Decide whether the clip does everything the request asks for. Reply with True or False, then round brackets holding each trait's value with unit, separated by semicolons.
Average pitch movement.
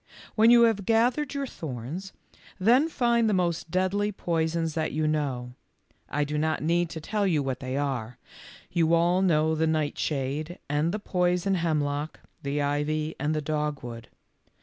True (4.2 semitones)